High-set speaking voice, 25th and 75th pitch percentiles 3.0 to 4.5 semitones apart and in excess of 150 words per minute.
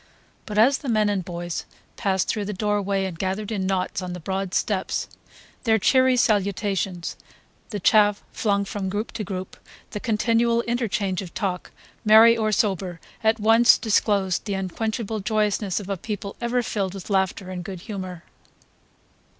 No: high, 205 Hz; narrow, 2.5 semitones; average, 160 wpm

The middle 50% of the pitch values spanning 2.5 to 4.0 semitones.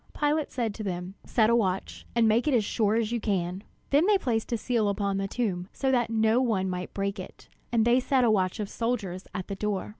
Yes: average, 3.4 semitones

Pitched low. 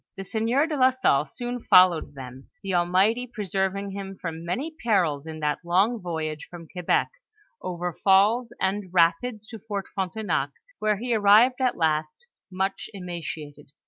No: high, 190 Hz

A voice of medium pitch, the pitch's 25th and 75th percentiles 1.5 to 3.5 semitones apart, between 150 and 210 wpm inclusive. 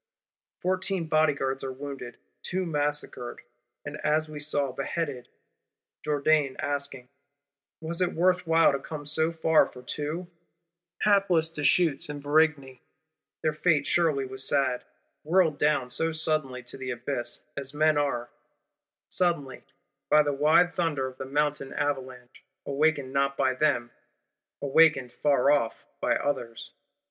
No: medium, 145 Hz; average, 2.9 semitones; slow, 135 wpm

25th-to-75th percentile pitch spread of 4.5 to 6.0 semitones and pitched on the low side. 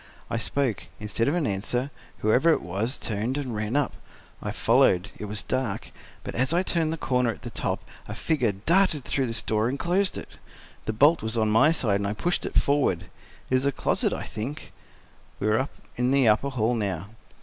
Yes: average, 4.9 semitones; low, 120 Hz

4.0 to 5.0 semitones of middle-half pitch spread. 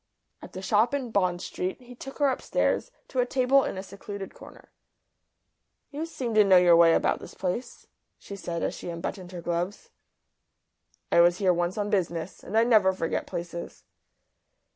No: wide, 5.4 semitones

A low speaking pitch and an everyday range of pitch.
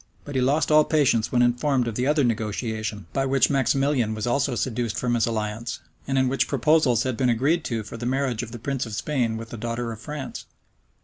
Yes: low, 125 Hz; average, 3.2 semitones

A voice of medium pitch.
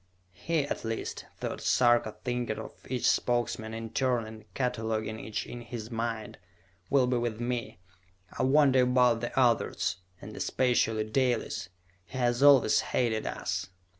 No: low, 120 Hz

